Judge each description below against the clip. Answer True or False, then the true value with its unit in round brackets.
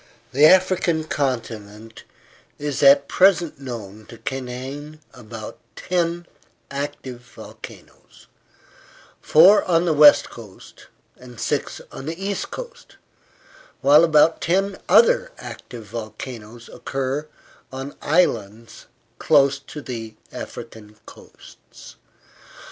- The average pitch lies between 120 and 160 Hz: True (140 Hz)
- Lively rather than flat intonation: True (5.7 semitones)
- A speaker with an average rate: False (100 wpm)